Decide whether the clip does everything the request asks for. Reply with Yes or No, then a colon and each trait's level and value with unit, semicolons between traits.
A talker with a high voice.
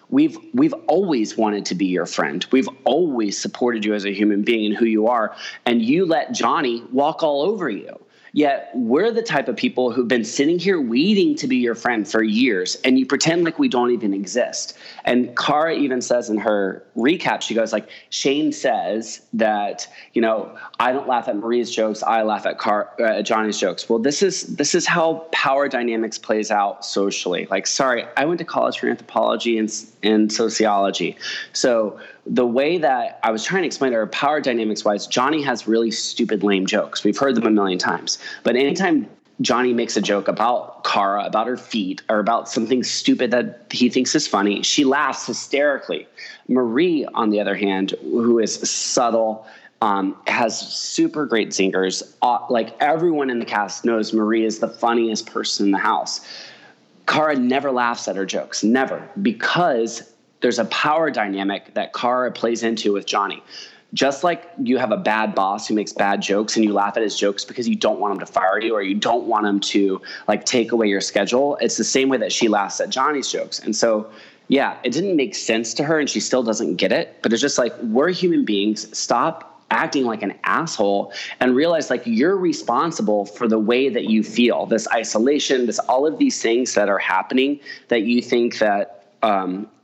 No: low, 115 Hz